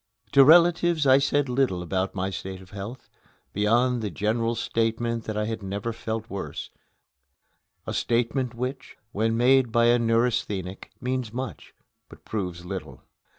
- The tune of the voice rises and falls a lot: No, average, 4.1 semitones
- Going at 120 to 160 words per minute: Yes, average, 150 wpm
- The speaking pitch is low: Yes, low, 115 Hz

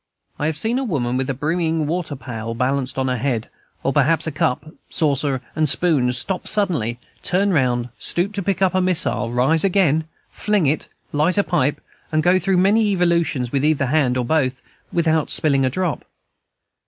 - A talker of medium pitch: Yes, medium, 155 Hz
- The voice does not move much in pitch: No, wide, 5.4 semitones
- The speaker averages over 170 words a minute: Yes, average, 185 wpm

